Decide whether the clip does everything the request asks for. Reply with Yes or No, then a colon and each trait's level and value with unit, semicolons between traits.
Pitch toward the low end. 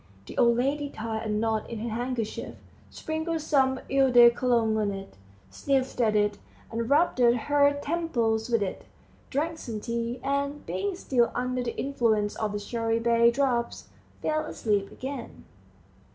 No: high, 240 Hz